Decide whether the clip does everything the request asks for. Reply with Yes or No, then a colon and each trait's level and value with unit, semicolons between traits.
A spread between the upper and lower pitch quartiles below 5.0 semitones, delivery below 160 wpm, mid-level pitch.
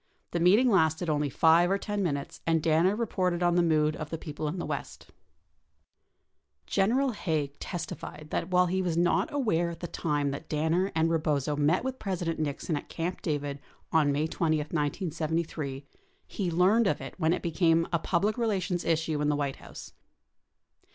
No: average, 3.1 semitones; average, 180 wpm; medium, 165 Hz